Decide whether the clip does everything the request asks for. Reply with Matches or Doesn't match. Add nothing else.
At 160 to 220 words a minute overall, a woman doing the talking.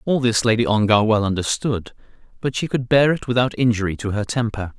Doesn't match